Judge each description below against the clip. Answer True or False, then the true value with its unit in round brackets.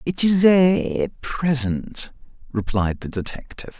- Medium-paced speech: False (110 wpm)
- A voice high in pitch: False (140 Hz)